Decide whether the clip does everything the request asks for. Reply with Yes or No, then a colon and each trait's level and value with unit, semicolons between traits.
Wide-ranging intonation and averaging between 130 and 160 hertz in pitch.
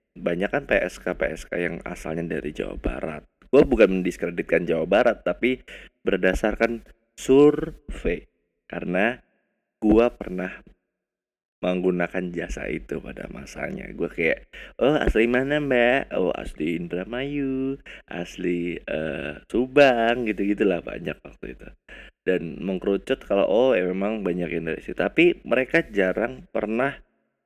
No: wide, 6.2 semitones; low, 105 Hz